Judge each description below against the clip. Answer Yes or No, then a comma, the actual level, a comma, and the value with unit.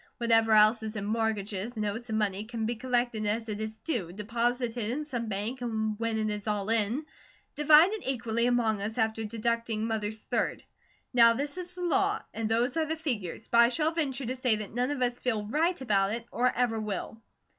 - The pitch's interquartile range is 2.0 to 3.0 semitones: Yes, narrow, 2.6 semitones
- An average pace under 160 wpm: No, fast, 205 wpm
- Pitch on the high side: Yes, high, 230 Hz